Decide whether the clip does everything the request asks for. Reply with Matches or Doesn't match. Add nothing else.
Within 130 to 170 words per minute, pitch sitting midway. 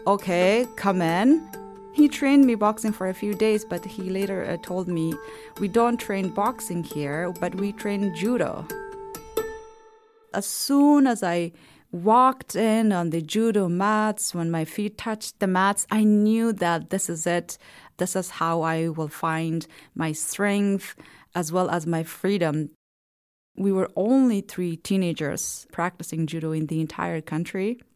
Doesn't match